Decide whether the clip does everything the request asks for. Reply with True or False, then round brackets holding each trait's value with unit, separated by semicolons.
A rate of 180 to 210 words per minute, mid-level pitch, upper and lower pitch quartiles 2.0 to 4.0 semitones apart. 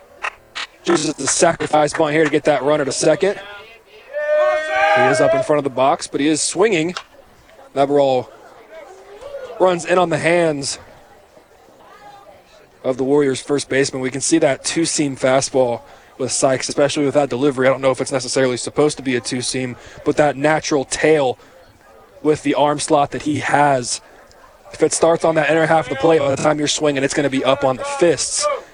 True (195 wpm; 150 Hz; 3.1 semitones)